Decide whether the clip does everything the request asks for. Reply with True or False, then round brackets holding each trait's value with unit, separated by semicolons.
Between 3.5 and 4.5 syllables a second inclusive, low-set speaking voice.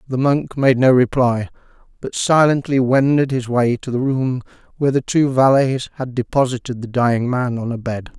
False (5.0 syllables/s; 130 Hz)